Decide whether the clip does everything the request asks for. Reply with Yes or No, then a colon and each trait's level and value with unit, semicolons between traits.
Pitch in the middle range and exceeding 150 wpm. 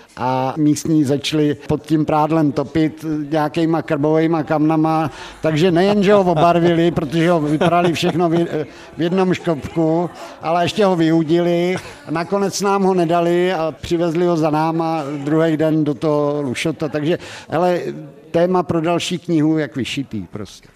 No: medium, 160 Hz; average, 140 wpm